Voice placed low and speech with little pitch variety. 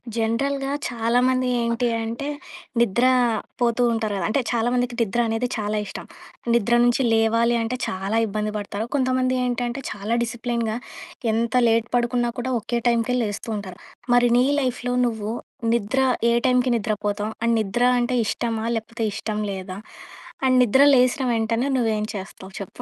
No: high, 235 Hz; narrow, 2.2 semitones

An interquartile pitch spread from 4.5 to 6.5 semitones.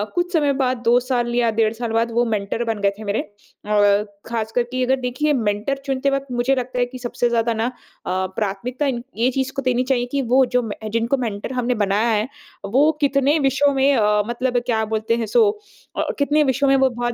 No: average, 3.3 semitones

